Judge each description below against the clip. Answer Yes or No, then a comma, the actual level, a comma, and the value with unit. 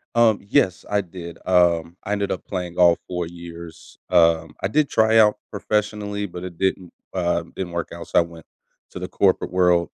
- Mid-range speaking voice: No, very low, 90 Hz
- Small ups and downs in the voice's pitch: No, average, 3.1 semitones